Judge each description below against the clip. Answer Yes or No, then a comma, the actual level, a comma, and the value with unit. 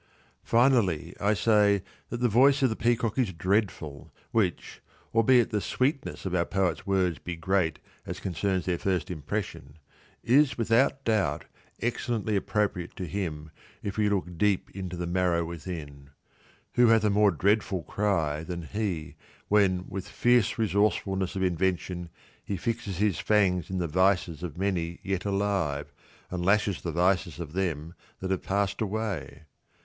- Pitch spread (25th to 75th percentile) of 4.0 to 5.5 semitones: No, average, 3.4 semitones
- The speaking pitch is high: No, very low, 95 Hz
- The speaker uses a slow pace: No, average, 155 wpm